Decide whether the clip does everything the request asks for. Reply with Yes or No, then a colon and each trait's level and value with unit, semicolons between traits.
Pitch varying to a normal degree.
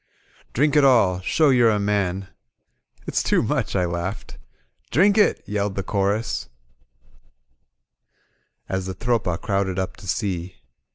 Yes: average, 3.8 semitones